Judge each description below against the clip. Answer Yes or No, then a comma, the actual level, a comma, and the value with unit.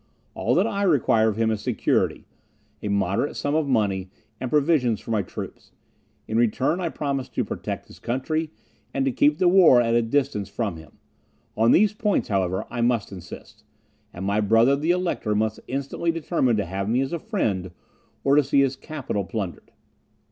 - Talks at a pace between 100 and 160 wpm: No, average, 185 wpm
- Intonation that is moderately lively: No, wide, 6.1 semitones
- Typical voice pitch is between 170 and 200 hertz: No, low, 120 Hz